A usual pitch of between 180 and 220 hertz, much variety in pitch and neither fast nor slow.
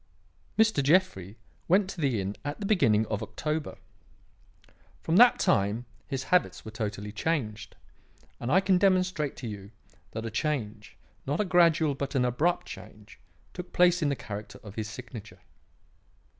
No: low, 135 Hz; wide, 8.4 semitones; average, 155 wpm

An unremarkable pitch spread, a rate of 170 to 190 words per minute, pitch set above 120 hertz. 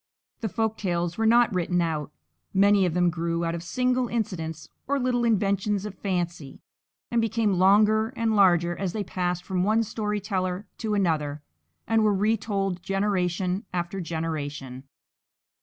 No: average, 3.9 semitones; average, 155 wpm; high, 190 Hz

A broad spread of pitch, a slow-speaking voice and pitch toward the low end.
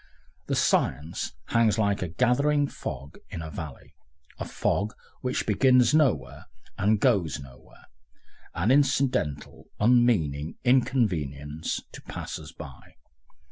Yes: wide, 8.5 semitones; slow, 110 wpm; low, 105 Hz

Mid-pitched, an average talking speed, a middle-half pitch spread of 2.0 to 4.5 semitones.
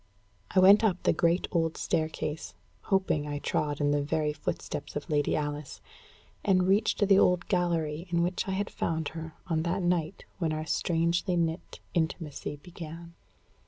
Yes: medium, 165 Hz; average, 160 wpm; average, 2.9 semitones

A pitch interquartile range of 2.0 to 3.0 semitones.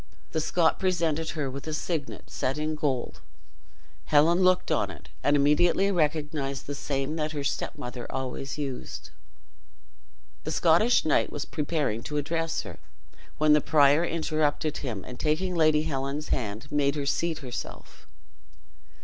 Yes: narrow, 2.4 semitones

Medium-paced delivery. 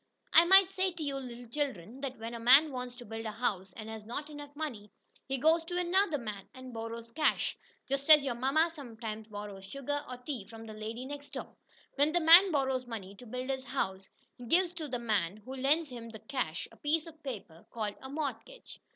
No: fast, 220 wpm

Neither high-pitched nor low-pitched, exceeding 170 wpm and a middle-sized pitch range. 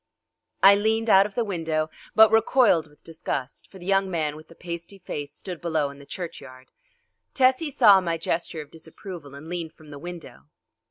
Yes: medium, 170 Hz; average, 185 wpm; average, 4.1 semitones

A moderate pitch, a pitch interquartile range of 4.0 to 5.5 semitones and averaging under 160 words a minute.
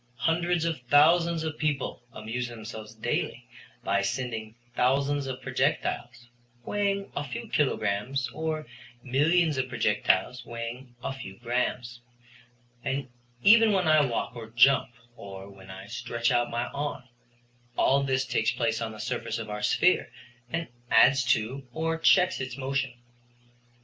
No: low, 130 Hz; average, 4.4 semitones; average, 140 wpm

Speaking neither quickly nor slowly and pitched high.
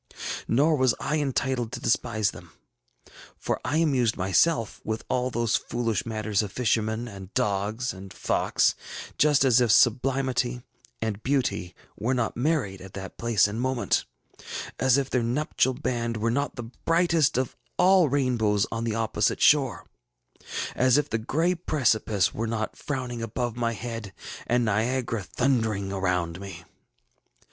No: average, 150 wpm; low, 120 Hz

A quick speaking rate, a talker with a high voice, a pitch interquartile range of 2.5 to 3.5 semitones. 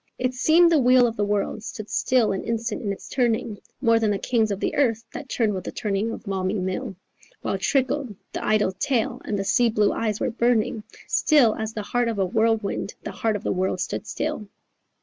Yes: fast, 220 wpm; high, 220 Hz; average, 2.9 semitones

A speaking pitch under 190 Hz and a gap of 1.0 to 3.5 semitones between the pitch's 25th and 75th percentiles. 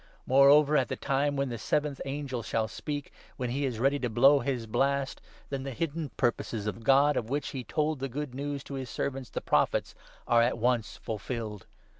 Yes: low, 135 Hz; average, 3.0 semitones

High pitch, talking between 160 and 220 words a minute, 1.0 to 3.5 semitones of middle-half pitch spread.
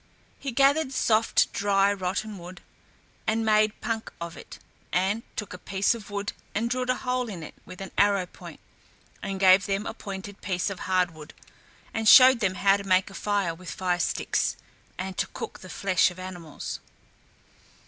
Yes: high, 195 Hz; average, 180 wpm; average, 2.9 semitones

